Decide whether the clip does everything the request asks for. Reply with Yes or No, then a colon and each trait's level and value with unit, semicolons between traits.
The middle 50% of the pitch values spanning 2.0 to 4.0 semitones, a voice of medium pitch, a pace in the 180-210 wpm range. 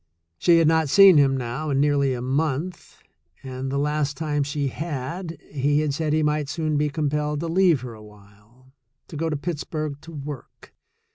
Yes: average, 2.7 semitones; medium, 145 Hz; average, 190 wpm